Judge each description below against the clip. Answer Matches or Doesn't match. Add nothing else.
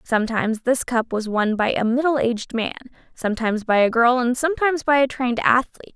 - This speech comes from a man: Doesn't match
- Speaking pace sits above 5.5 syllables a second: Matches